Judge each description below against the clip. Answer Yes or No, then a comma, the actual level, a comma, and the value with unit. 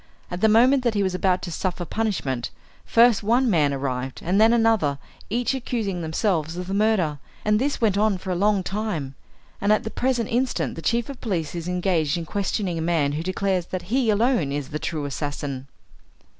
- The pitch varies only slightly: No, wide, 5.6 semitones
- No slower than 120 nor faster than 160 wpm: No, average, 200 wpm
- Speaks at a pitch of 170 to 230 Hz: Yes, high, 190 Hz